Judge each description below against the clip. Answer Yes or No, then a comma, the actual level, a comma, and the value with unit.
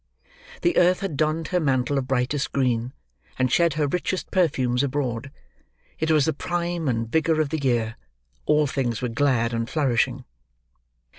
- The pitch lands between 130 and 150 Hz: Yes, medium, 140 Hz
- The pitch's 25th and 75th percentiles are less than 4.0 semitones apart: No, average, 4.3 semitones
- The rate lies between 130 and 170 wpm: Yes, average, 160 wpm